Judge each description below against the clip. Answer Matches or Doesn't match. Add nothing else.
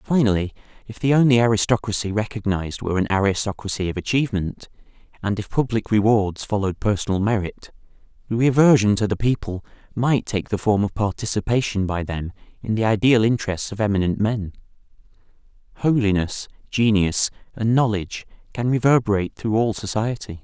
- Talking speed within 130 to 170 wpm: Matches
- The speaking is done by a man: Matches